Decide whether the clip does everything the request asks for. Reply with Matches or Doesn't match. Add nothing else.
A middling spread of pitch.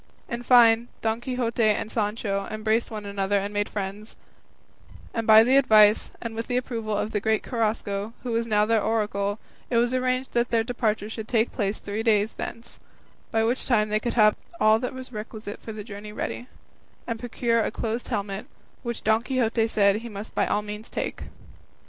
Doesn't match